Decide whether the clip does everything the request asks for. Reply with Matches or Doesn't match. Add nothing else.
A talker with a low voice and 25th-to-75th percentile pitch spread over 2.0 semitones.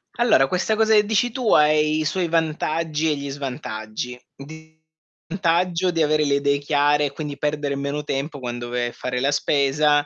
Doesn't match